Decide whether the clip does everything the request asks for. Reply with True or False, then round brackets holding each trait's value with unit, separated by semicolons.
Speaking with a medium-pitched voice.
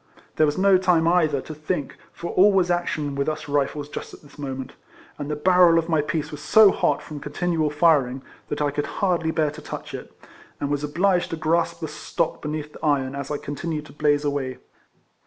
True (150 Hz)